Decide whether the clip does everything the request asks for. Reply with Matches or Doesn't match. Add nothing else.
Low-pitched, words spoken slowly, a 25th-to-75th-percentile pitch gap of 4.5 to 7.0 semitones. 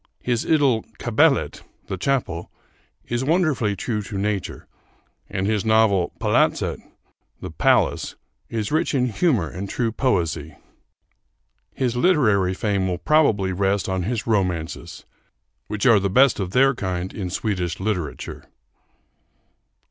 Matches